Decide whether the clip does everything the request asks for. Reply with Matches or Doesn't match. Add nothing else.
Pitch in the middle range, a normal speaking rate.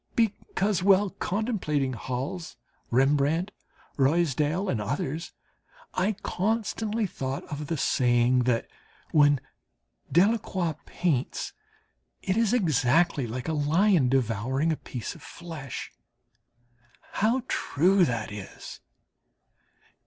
Doesn't match